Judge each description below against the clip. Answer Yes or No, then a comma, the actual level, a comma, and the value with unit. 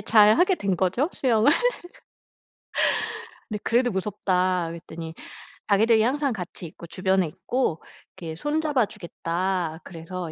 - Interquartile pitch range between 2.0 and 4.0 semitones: No, average, 5.1 semitones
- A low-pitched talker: No, high, 190 Hz